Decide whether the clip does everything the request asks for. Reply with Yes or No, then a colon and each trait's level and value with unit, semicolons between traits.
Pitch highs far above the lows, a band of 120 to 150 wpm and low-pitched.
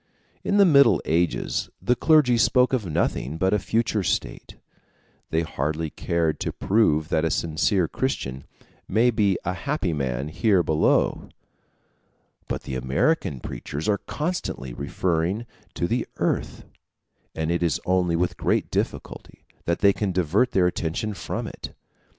Yes: wide, 5.8 semitones; average, 145 wpm; very low, 90 Hz